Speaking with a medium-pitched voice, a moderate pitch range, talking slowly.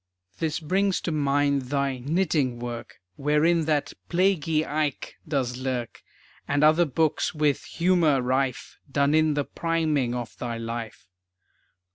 Yes: medium, 145 Hz; average, 3.6 semitones; slow, 130 wpm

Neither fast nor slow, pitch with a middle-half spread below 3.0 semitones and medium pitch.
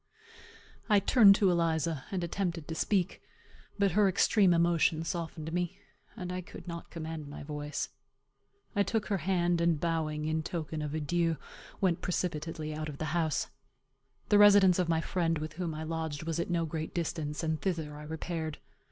Yes: average, 180 wpm; narrow, 2.4 semitones; medium, 165 Hz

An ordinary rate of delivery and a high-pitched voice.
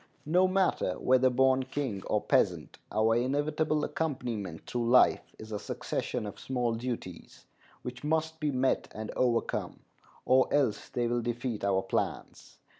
No: average, 145 wpm; low, 125 Hz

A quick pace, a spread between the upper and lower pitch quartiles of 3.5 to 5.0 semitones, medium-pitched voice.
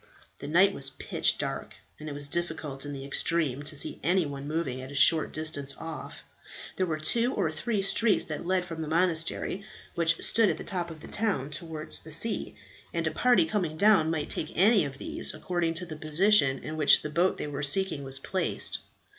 Yes: fast, 210 wpm; average, 3.9 semitones; medium, 160 Hz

